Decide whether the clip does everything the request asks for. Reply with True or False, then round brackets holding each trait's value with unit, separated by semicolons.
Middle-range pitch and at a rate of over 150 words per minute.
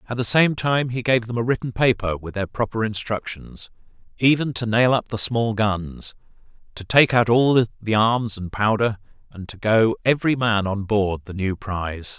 False (110 Hz; 190 wpm)